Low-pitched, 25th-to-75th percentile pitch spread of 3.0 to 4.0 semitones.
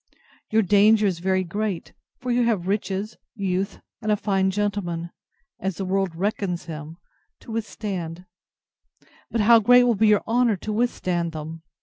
No: high, 200 Hz; average, 3.3 semitones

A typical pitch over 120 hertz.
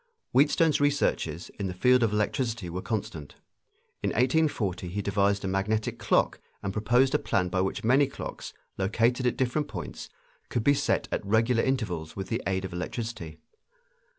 No: low, 110 Hz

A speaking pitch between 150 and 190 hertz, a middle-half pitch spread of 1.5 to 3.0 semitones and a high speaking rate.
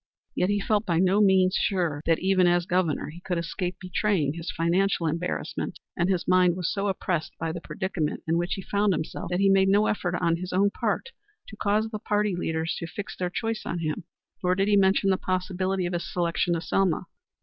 Yes: medium, 185 Hz; narrow, 2.4 semitones; fast, 215 wpm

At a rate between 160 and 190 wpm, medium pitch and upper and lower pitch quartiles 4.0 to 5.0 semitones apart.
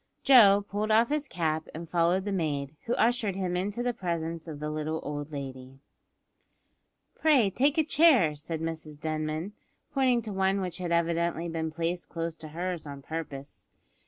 Yes: average, 170 wpm; medium, 170 Hz; average, 4.6 semitones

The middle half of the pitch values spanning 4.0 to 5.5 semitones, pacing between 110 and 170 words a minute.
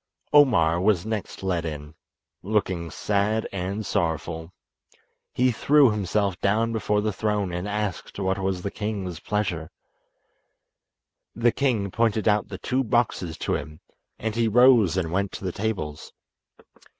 No: average, 3.6 semitones; average, 140 wpm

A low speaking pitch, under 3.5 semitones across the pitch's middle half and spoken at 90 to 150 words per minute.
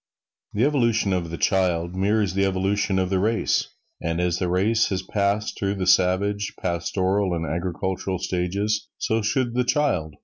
No: very low, 95 Hz; narrow, 2.6 semitones; average, 165 wpm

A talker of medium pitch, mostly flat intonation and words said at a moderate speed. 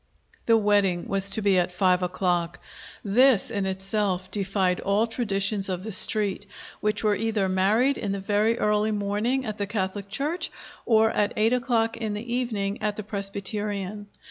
No: high, 205 Hz; narrow, 2.2 semitones; average, 170 wpm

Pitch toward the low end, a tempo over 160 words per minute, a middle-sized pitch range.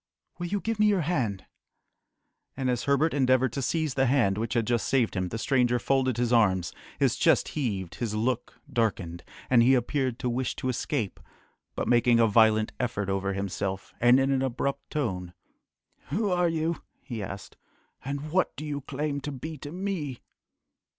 Yes: low, 125 Hz; average, 180 wpm; average, 4.3 semitones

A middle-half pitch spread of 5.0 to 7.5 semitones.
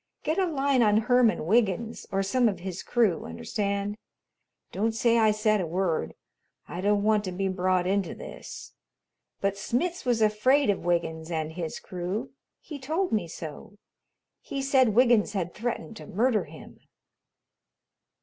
No: average, 4.6 semitones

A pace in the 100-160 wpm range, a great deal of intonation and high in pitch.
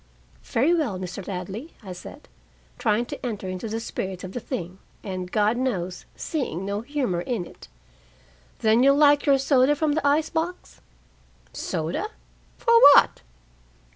Yes: average, 150 wpm; wide, 7.4 semitones; high, 230 Hz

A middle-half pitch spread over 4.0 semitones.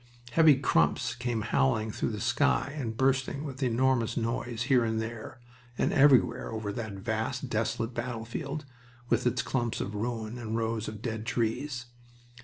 No: average, 2.7 semitones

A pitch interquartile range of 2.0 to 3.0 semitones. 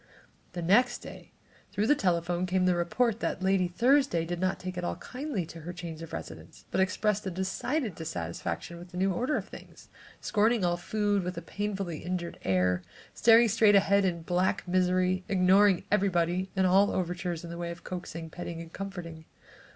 Yes: average, 2.7 semitones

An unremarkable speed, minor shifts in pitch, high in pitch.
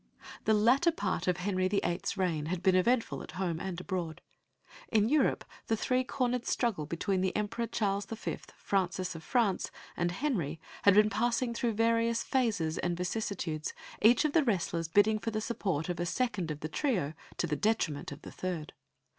No: average, 180 wpm; average, 4.9 semitones; high, 200 Hz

